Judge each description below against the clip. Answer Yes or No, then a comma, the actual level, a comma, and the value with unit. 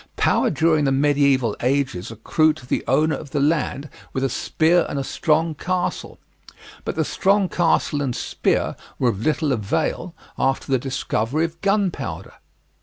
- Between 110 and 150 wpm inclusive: No, average, 160 wpm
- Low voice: No, medium, 145 Hz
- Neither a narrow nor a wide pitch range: Yes, average, 3.5 semitones